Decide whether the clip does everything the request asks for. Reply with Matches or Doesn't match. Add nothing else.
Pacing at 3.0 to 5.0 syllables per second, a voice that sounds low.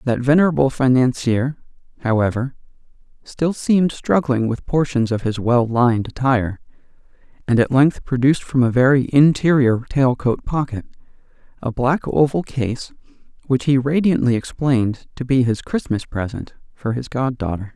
Matches